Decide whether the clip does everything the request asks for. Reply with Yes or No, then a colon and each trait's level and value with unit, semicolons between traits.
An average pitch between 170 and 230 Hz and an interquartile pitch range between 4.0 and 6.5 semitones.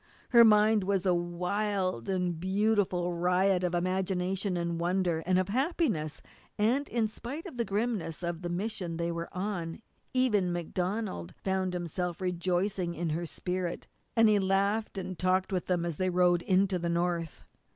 No: medium, 185 Hz; average, 2.7 semitones